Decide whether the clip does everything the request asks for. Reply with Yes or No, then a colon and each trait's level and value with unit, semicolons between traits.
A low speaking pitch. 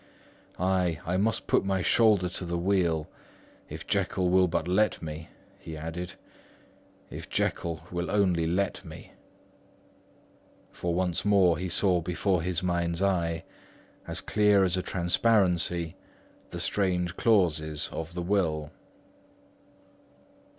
Yes: very low, 90 Hz